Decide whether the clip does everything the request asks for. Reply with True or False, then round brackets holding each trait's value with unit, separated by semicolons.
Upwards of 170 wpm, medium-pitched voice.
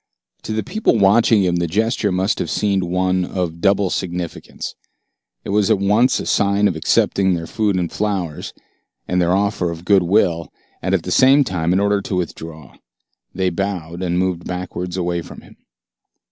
False (185 wpm; 95 Hz)